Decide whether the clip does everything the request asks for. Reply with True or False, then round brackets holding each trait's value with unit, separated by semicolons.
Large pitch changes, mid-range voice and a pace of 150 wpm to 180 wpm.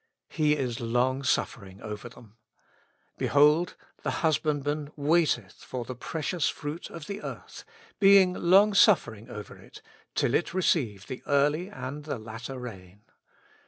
False (5.7 semitones; 145 Hz; 135 wpm)